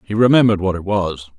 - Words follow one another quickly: Yes, fast, 215 wpm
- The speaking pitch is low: Yes, low, 100 Hz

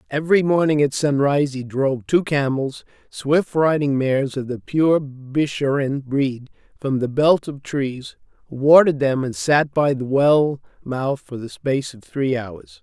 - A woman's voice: No, male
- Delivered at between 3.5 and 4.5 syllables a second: Yes, 4.2 syllables/s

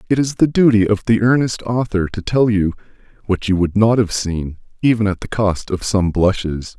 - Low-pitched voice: Yes, low, 105 Hz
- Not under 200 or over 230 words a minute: Yes, fast, 205 wpm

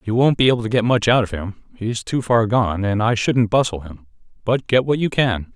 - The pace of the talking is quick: Yes, fast, 250 wpm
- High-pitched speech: No, low, 115 Hz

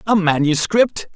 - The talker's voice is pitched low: No, medium, 180 Hz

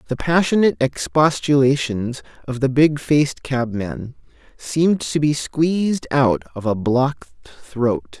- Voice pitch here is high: No, medium, 140 Hz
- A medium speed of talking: No, slow, 125 wpm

